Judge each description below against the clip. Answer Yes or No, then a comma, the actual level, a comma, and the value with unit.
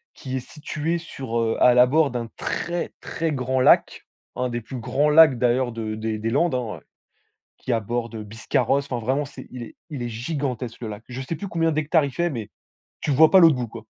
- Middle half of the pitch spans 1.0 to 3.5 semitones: No, average, 4.3 semitones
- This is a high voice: No, low, 130 Hz